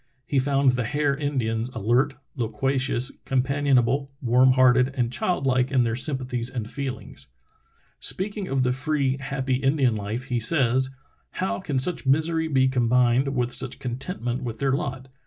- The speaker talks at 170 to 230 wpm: No, average, 155 wpm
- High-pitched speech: No, low, 130 Hz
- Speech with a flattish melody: Yes, narrow, 2.0 semitones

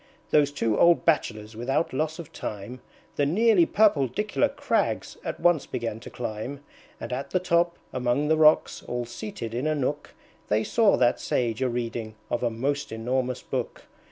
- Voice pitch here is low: Yes, low, 130 Hz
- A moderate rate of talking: Yes, average, 170 wpm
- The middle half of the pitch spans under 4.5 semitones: No, average, 5.1 semitones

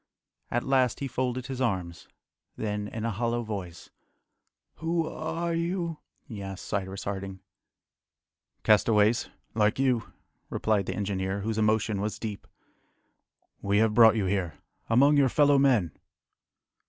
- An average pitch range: Yes, average, 4.5 semitones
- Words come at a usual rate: No, slow, 130 wpm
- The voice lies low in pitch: Yes, low, 110 Hz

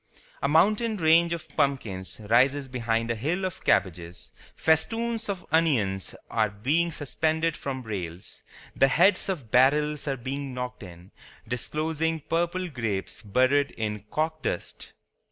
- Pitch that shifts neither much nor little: No, wide, 6.1 semitones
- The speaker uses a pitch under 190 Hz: Yes, medium, 140 Hz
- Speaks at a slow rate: Yes, slow, 130 wpm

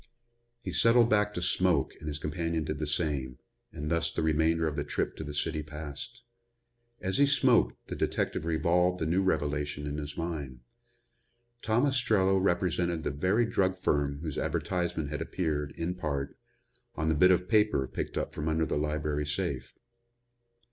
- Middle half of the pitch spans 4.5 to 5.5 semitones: No, average, 3.8 semitones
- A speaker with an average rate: Yes, average, 170 wpm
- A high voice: No, very low, 80 Hz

